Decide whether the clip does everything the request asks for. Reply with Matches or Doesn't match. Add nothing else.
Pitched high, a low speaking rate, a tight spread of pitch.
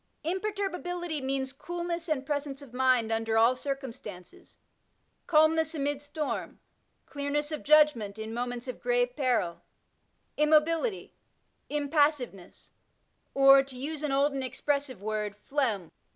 Doesn't match